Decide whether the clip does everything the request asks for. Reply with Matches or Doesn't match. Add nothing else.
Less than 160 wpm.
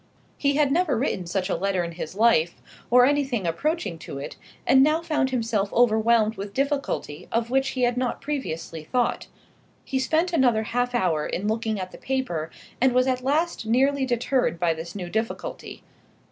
Doesn't match